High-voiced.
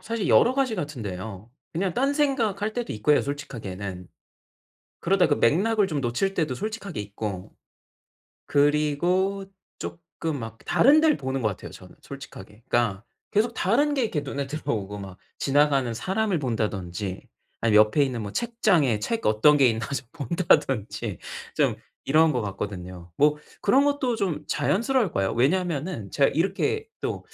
No: medium, 145 Hz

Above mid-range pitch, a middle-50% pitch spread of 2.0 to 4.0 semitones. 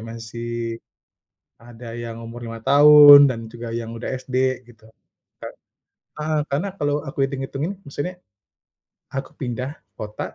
No: low, 125 Hz; average, 3.7 semitones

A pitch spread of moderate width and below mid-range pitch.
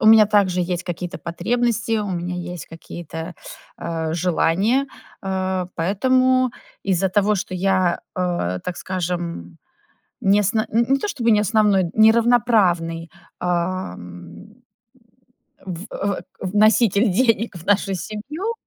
No: average, 3.9 semitones; high, 190 Hz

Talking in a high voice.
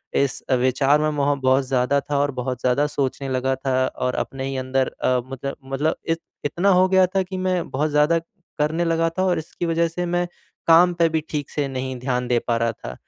No: medium, 145 Hz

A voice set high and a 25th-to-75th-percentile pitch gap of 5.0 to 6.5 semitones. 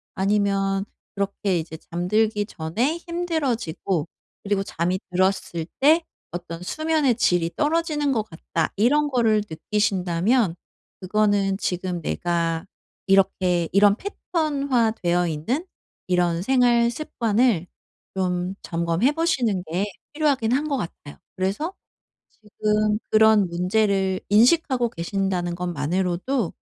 Yes: high, 200 Hz; wide, 5.6 semitones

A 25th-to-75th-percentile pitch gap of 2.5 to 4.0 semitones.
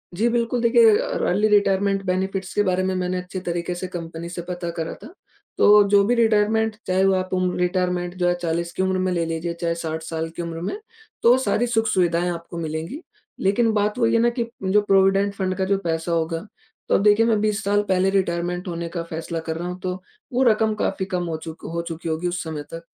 Yes: average, 3.3 semitones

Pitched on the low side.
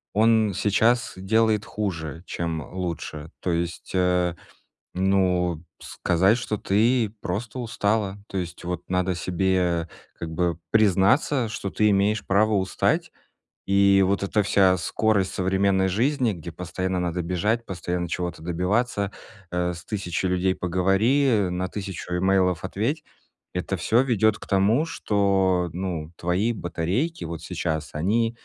Yes: very low, 95 Hz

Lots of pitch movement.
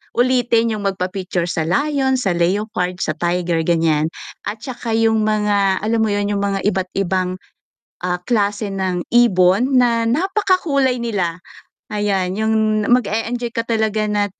No: average, 3.9 semitones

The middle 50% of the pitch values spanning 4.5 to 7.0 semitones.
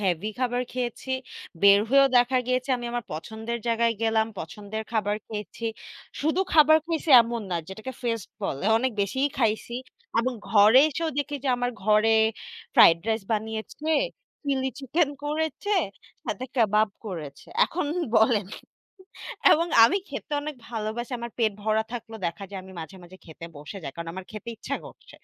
No: average, 3.9 semitones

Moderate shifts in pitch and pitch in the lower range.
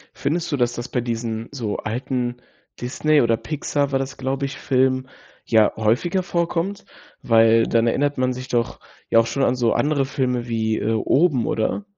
Yes: average, 3.5 semitones; low, 125 Hz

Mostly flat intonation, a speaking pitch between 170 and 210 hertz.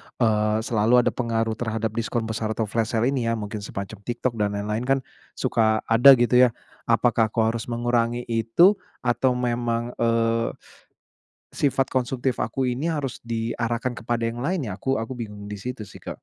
No: narrow, 1.8 semitones; low, 115 Hz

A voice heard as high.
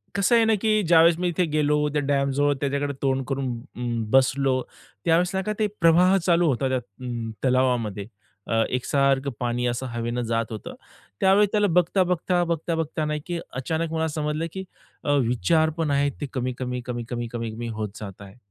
No: medium, 140 Hz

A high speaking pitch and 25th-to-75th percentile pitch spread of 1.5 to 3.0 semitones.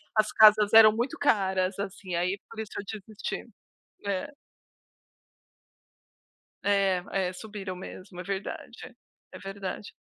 Yes: high, 200 Hz; narrow, 2.4 semitones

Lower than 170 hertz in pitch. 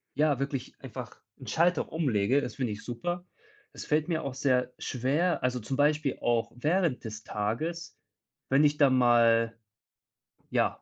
Yes: low, 135 Hz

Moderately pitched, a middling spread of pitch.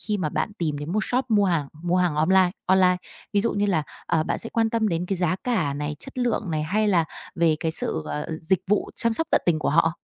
Yes: medium, 180 Hz; average, 4.8 semitones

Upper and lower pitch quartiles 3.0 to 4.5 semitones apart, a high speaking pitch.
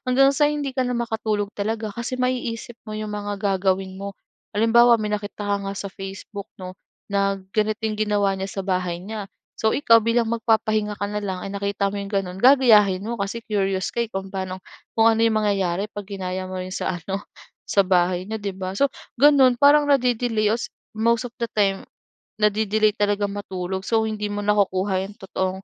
No: narrow, 2.6 semitones; high, 205 Hz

